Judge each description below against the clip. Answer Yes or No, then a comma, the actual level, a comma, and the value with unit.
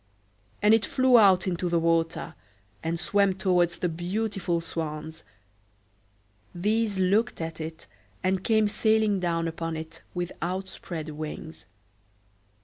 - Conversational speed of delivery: No, slow, 125 wpm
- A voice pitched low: No, medium, 175 Hz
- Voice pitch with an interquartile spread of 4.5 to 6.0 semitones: No, average, 3.5 semitones